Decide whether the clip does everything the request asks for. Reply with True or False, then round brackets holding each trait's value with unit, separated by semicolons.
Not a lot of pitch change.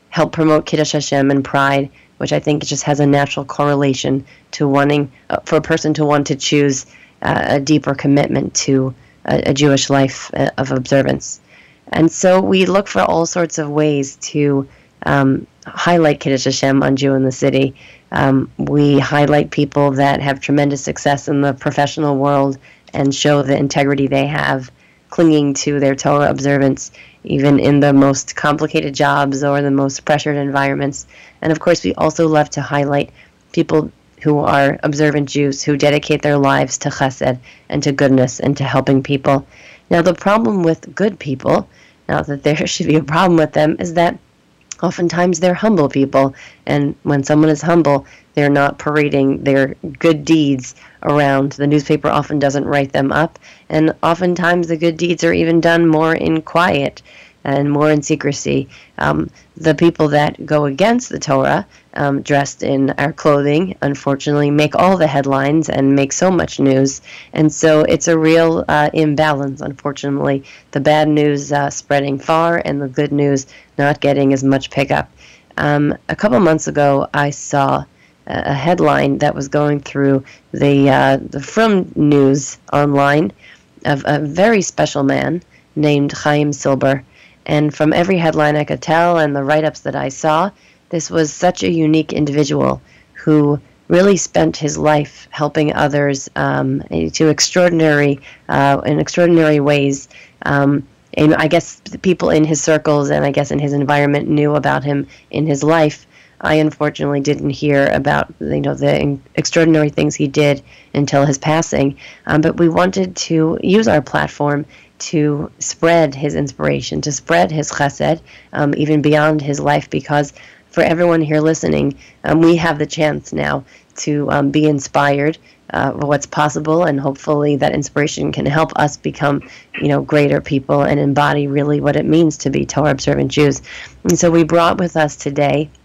True (1.9 semitones)